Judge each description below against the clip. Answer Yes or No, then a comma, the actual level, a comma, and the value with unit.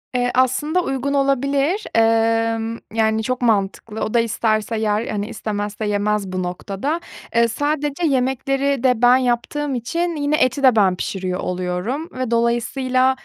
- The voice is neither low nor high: No, high, 240 Hz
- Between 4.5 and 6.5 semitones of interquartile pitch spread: No, average, 4.0 semitones